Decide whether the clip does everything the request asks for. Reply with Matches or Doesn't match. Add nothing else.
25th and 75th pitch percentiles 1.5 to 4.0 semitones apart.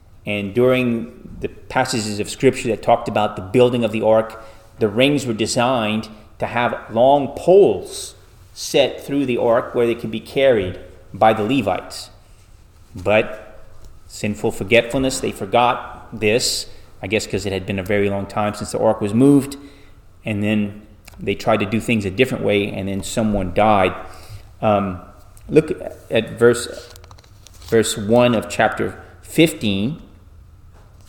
Matches